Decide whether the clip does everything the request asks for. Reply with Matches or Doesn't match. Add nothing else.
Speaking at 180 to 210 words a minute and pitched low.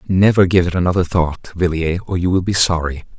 Matches